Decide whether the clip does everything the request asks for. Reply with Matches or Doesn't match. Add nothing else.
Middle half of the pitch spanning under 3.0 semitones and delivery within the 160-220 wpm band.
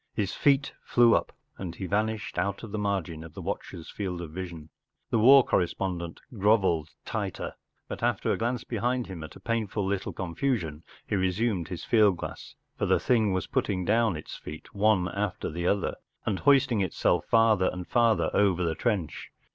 Doesn't match